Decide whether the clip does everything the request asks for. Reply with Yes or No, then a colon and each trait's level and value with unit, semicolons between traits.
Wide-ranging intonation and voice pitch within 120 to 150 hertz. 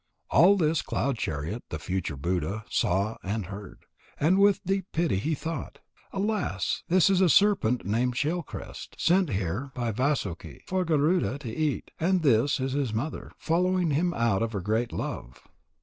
Yes: wide, 8.5 semitones; low, 135 Hz